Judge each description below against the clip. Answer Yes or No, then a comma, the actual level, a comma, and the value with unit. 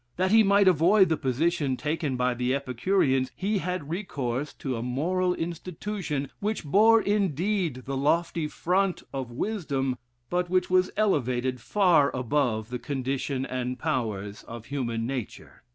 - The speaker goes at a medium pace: Yes, average, 145 wpm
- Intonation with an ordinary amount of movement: No, wide, 6.3 semitones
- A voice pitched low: No, medium, 150 Hz